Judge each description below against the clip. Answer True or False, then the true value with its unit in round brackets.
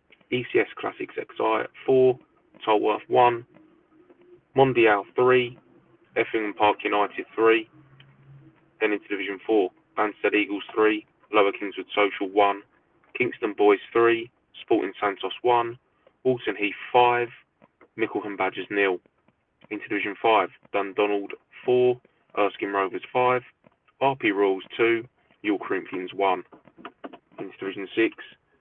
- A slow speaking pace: True (110 wpm)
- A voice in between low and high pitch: False (125 Hz)